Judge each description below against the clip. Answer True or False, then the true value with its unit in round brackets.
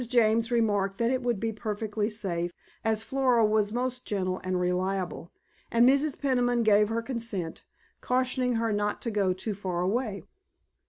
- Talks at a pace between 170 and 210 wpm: False (160 wpm)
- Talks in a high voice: True (220 Hz)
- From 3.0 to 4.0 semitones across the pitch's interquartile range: True (3.6 semitones)